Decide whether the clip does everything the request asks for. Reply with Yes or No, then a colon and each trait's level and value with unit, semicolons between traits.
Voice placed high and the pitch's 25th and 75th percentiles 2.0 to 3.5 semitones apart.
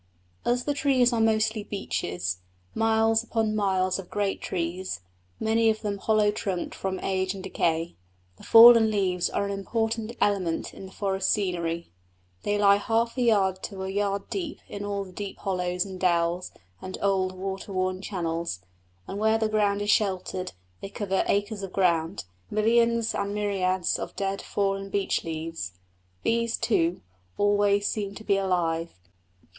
Yes: high, 200 Hz; average, 2.7 semitones